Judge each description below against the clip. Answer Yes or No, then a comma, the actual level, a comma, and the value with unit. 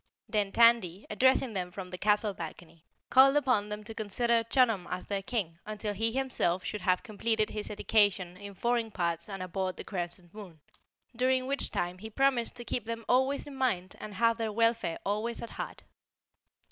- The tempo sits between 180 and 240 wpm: Yes, average, 185 wpm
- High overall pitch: Yes, high, 215 Hz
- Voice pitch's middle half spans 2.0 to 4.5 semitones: Yes, average, 4.1 semitones